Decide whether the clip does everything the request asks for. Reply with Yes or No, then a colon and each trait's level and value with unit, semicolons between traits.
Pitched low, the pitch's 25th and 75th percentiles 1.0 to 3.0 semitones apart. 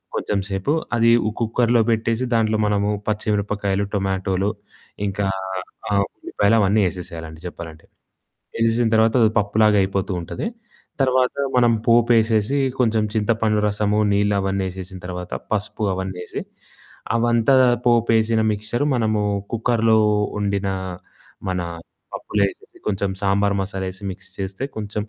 Yes: low, 105 Hz; narrow, 2.6 semitones